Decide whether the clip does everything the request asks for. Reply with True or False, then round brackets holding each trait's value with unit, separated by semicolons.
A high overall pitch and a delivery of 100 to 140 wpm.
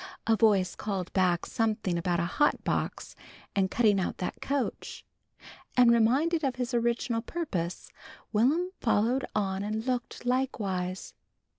True (225 Hz; 135 wpm)